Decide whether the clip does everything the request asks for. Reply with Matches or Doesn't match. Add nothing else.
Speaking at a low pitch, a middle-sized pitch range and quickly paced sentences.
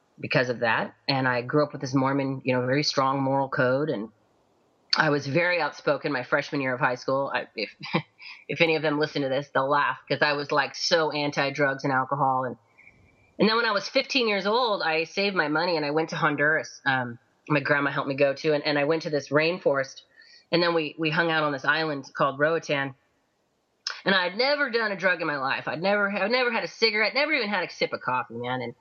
Doesn't match